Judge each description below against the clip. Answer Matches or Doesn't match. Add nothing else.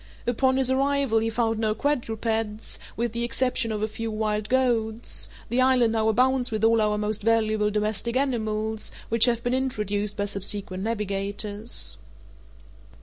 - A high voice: Matches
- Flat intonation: Matches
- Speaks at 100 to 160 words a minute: Matches